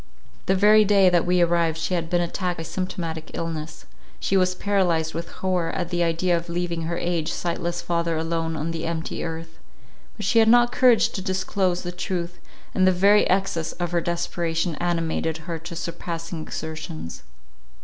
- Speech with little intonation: Yes, narrow, 2.0 semitones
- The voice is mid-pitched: Yes, medium, 170 Hz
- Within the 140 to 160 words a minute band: No, average, 180 wpm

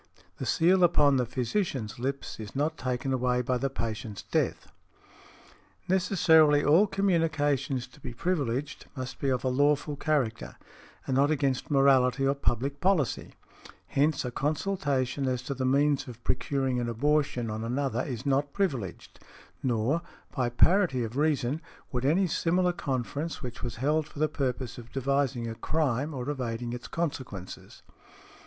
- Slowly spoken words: No, average, 150 wpm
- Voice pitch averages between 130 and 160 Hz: Yes, low, 135 Hz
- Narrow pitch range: No, average, 3.4 semitones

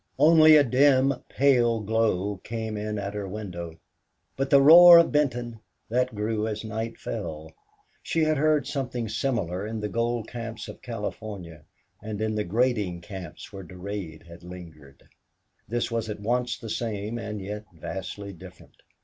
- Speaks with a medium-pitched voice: No, low, 110 Hz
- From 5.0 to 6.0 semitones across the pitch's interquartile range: No, average, 3.7 semitones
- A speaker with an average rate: Yes, average, 160 wpm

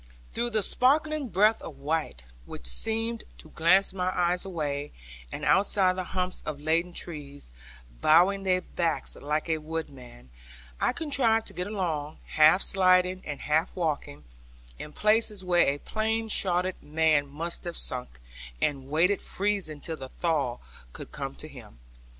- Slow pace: No, average, 150 wpm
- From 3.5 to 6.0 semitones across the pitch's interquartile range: Yes, average, 4.6 semitones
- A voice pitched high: No, medium, 175 Hz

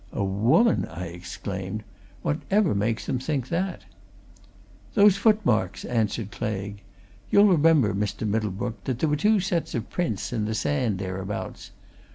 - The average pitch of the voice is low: Yes, low, 115 Hz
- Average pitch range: No, wide, 8.1 semitones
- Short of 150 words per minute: Yes, average, 140 wpm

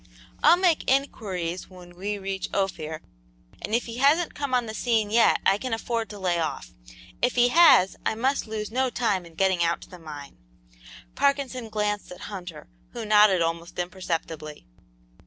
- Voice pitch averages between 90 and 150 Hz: No, high, 205 Hz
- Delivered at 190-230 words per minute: No, average, 175 wpm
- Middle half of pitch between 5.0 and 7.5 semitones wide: Yes, wide, 5.5 semitones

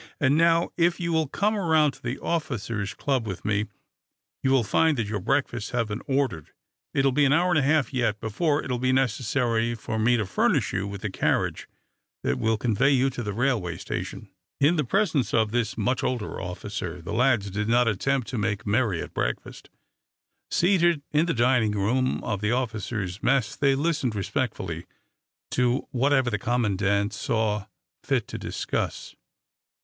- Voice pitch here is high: No, low, 120 Hz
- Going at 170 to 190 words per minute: Yes, average, 185 wpm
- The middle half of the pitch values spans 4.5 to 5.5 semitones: Yes, average, 4.8 semitones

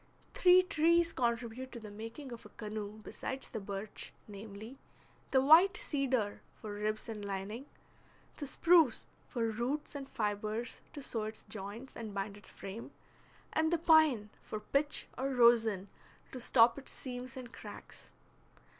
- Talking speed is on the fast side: No, average, 150 wpm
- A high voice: Yes, high, 235 Hz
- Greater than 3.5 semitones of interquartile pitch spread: Yes, average, 4.4 semitones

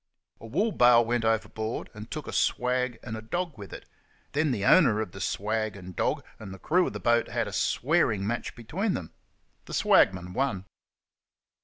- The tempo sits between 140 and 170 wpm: No, average, 190 wpm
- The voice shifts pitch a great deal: No, average, 4.3 semitones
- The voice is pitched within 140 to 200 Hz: No, low, 115 Hz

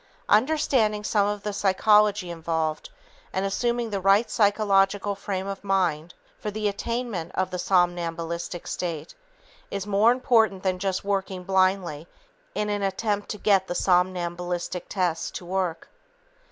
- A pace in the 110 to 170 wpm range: Yes, average, 140 wpm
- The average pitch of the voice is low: No, high, 195 Hz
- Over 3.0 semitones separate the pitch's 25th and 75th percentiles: No, average, 2.7 semitones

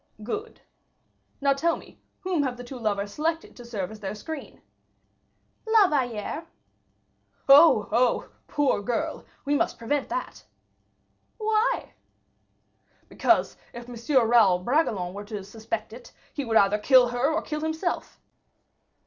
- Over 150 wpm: No, slow, 135 wpm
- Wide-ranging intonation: Yes, wide, 6.0 semitones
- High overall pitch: Yes, high, 245 Hz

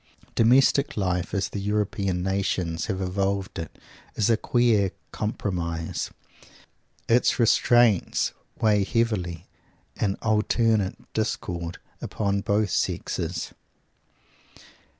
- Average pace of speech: No, slow, 90 wpm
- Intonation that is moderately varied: Yes, average, 3.2 semitones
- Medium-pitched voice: No, low, 100 Hz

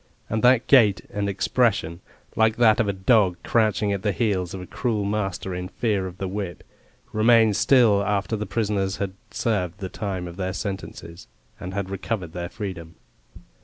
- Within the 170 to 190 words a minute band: Yes, average, 175 wpm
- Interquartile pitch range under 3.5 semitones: Yes, average, 2.8 semitones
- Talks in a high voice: No, low, 100 Hz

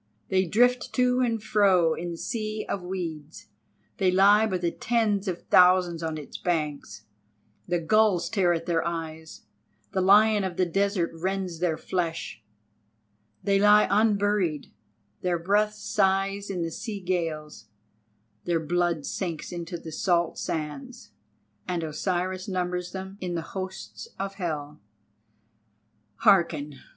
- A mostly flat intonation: No, average, 3.2 semitones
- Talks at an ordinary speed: No, slow, 130 wpm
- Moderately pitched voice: Yes, medium, 180 Hz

